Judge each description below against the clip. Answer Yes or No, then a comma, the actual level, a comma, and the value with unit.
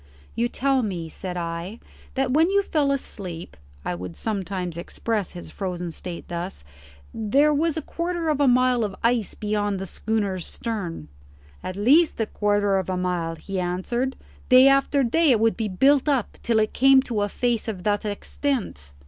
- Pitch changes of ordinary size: No, wide, 6.3 semitones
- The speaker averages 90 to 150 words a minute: No, average, 180 wpm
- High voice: Yes, high, 215 Hz